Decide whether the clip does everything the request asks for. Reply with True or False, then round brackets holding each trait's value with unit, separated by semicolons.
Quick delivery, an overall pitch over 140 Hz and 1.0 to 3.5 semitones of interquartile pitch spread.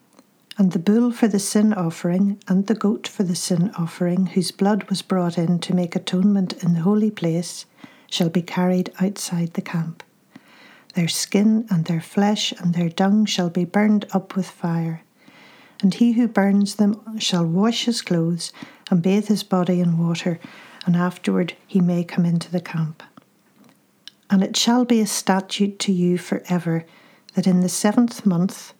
False (175 wpm; 190 Hz; 3.1 semitones)